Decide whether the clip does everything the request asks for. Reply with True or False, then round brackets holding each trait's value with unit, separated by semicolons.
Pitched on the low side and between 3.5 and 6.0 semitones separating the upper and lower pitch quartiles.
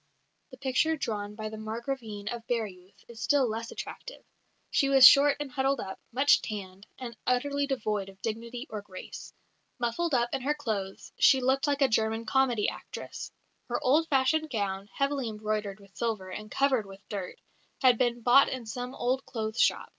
False (235 Hz; 4.0 semitones)